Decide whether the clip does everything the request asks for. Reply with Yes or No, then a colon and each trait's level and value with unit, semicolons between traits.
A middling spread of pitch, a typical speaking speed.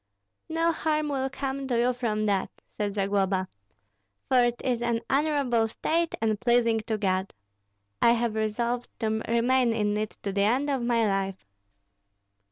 Yes: average, 3.6 semitones; average, 160 wpm